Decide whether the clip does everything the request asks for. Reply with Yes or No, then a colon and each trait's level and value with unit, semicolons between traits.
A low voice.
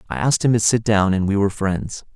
Yes: low, 105 Hz